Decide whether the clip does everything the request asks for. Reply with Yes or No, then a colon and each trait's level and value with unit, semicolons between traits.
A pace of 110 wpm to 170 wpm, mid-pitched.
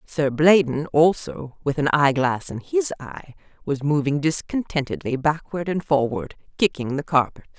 Yes: average, 140 wpm; medium, 145 Hz